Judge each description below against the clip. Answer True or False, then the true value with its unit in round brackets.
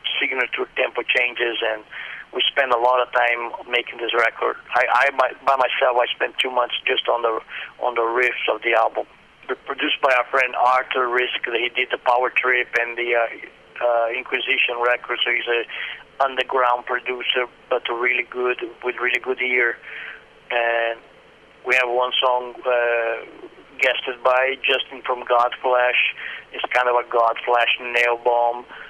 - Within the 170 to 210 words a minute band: False (160 wpm)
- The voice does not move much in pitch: True (1.0 semitones)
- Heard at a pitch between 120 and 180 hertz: True (125 Hz)